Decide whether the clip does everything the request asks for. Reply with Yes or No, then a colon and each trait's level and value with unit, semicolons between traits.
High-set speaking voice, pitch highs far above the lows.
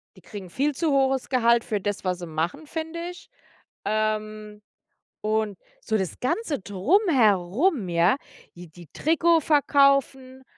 Yes: high, 235 Hz; wide, 6.3 semitones